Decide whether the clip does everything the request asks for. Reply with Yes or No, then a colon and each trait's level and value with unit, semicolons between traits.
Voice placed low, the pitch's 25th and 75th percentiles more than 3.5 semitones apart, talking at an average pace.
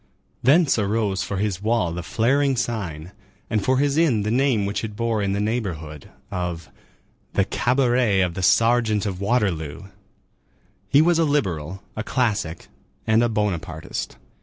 Yes: low, 105 Hz; average, 4.6 semitones; average, 155 wpm